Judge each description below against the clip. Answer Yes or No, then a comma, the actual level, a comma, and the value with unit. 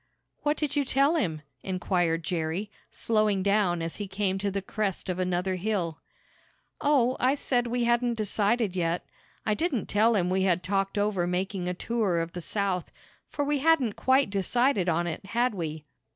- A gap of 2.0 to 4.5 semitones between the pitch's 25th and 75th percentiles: No, average, 4.9 semitones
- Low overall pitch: No, high, 200 Hz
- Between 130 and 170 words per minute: No, average, 180 wpm